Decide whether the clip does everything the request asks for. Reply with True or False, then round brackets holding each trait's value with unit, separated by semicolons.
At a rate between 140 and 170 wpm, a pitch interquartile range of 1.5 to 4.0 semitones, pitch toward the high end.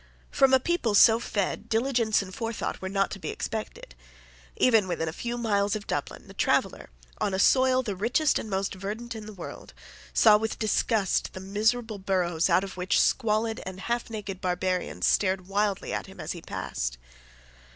False (185 wpm; 3.2 semitones; 210 Hz)